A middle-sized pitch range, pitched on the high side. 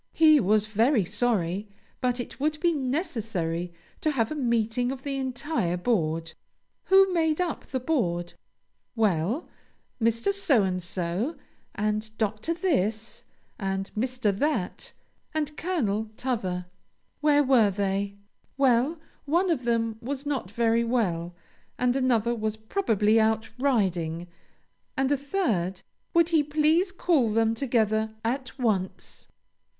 No: wide, 5.7 semitones; high, 230 Hz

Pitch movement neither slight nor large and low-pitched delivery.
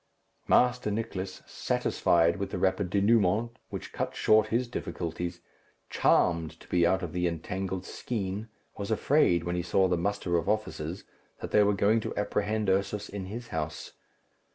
Yes: average, 3.3 semitones; very low, 95 Hz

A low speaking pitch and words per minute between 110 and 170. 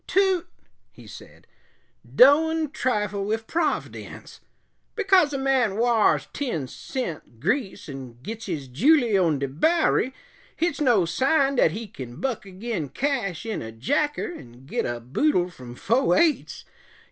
No: high, 225 Hz; average, 140 wpm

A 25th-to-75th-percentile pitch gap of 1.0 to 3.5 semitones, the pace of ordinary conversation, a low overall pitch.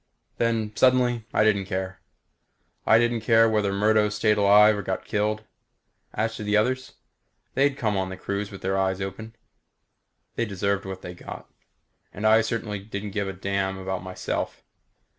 Yes: narrow, 2.4 semitones; average, 165 wpm; low, 105 Hz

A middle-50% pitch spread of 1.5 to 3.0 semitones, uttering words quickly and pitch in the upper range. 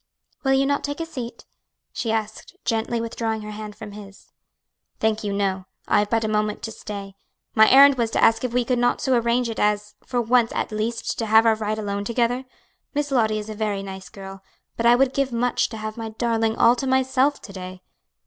Yes: narrow, 2.6 semitones; fast, 225 wpm; high, 225 Hz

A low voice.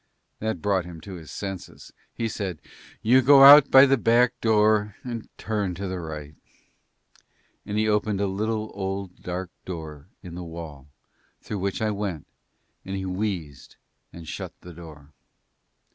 Yes: very low, 95 Hz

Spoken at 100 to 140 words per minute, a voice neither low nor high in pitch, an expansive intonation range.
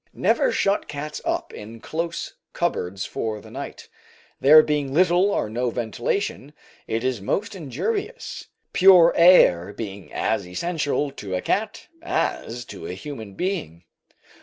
Yes: slow, 135 wpm; medium, 145 Hz; wide, 8.6 semitones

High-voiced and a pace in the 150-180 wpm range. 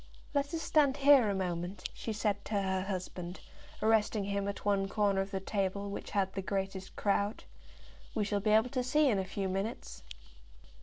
No: high, 200 Hz; average, 190 wpm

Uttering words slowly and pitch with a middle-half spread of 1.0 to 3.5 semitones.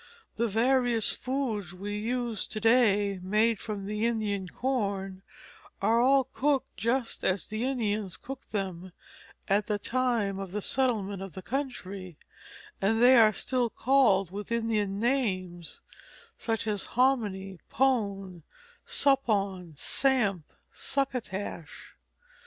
No: slow, 120 wpm; average, 4.1 semitones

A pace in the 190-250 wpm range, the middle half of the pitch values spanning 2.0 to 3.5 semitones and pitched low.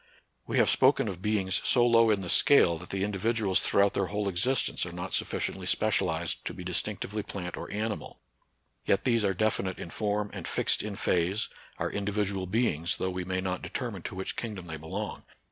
Yes: average, 195 wpm; average, 2.7 semitones; low, 100 Hz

